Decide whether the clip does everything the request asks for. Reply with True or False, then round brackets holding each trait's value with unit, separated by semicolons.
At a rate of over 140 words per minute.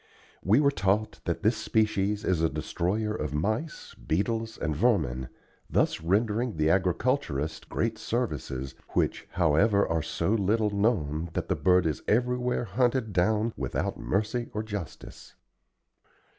False (135 wpm)